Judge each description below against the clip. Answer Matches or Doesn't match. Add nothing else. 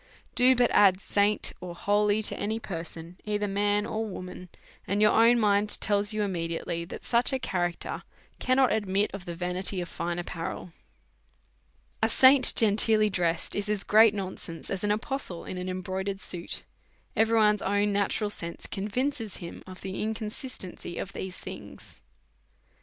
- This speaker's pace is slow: Doesn't match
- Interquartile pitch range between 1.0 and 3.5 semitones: Matches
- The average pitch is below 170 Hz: Doesn't match